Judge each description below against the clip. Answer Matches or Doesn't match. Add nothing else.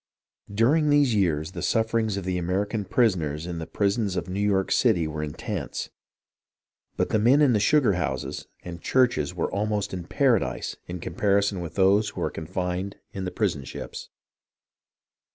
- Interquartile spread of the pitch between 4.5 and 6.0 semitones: Doesn't match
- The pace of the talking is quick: Doesn't match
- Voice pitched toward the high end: Doesn't match